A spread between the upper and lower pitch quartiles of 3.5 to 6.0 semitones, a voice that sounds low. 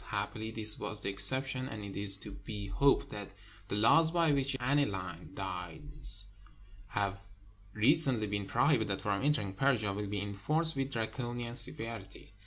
Yes: average, 5.2 semitones; low, 110 Hz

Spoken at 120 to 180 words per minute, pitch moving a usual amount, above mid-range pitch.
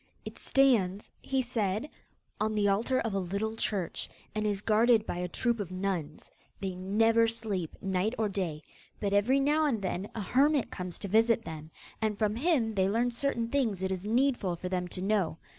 No: average, 195 wpm; average, 3.6 semitones; high, 210 Hz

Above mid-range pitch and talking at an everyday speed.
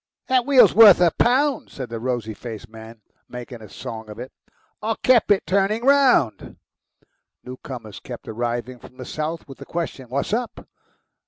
No: low, 130 Hz; average, 165 wpm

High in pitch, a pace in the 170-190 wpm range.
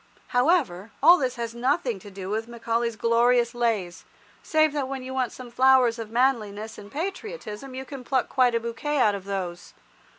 Yes: high, 240 Hz; average, 185 wpm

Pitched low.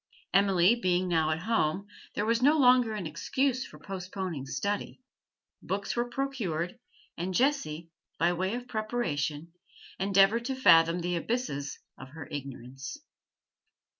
No: high, 190 Hz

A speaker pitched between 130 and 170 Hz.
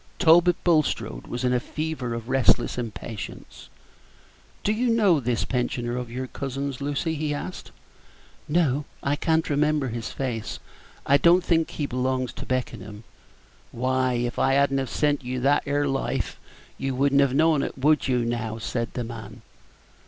Yes: low, 135 Hz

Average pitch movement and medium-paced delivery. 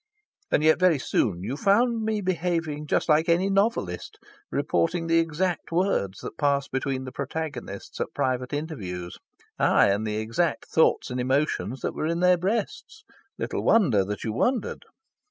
No: wide, 6.3 semitones; average, 160 wpm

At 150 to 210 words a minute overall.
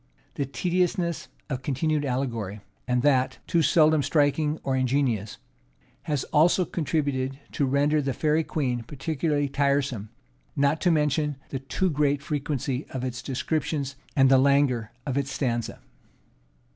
No: slow, 135 wpm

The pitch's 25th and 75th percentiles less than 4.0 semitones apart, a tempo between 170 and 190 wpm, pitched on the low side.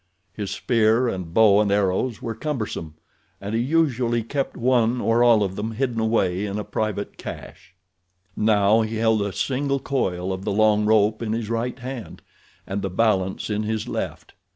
Yes: narrow, 2.6 semitones; average, 175 wpm; low, 110 Hz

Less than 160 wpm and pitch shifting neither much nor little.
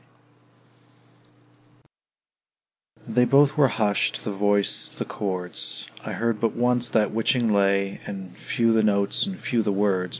Yes: slow, 135 wpm; average, 3.0 semitones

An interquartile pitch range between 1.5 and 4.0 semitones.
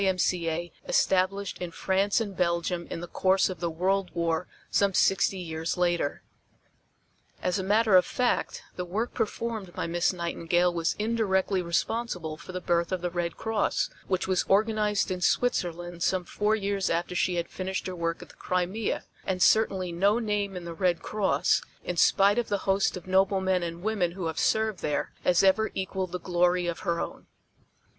Yes: narrow, 2.5 semitones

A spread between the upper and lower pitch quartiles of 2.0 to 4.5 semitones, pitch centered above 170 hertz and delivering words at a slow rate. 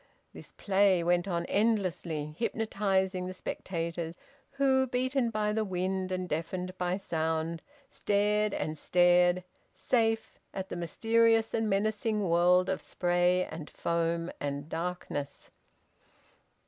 Yes: average, 3.7 semitones; medium, 185 Hz; slow, 120 wpm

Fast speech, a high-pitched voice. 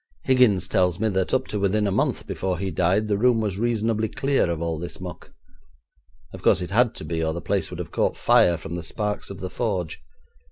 No: fast, 230 wpm; very low, 95 Hz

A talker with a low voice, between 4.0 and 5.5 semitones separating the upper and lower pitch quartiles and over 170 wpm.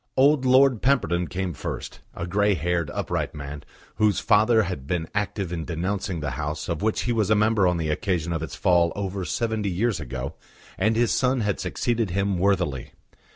Yes: very low, 95 Hz; average, 4.4 semitones; average, 190 wpm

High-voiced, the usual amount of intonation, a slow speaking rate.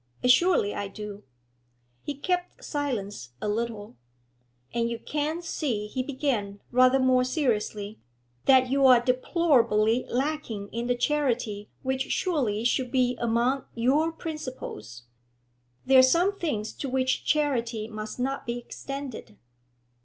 Yes: very high, 250 Hz; average, 4.2 semitones; slow, 130 wpm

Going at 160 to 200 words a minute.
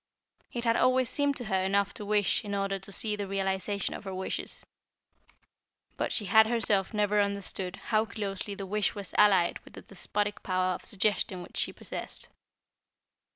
Yes: average, 175 wpm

